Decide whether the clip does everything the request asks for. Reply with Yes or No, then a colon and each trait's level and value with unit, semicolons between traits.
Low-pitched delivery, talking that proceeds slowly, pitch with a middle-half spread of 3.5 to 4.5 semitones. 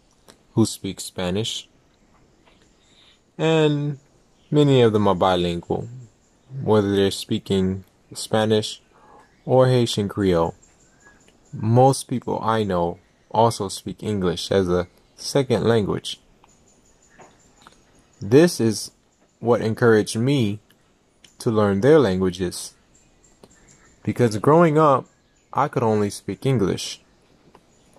Yes: low, 110 Hz; slow, 95 wpm; average, 4.2 semitones